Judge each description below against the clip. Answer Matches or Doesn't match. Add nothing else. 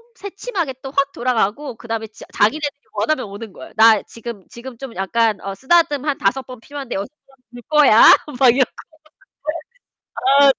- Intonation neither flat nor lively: Matches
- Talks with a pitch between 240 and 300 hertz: Matches